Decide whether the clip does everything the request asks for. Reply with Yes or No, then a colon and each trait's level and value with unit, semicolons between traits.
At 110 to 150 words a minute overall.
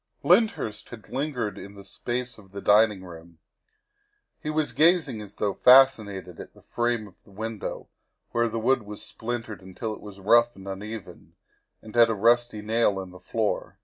No: average, 185 wpm